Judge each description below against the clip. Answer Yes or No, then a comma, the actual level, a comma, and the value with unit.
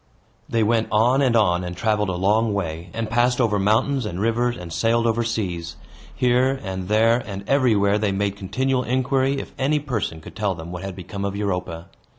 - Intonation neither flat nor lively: Yes, average, 4.1 semitones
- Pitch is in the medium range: No, low, 105 Hz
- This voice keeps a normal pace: Yes, average, 195 wpm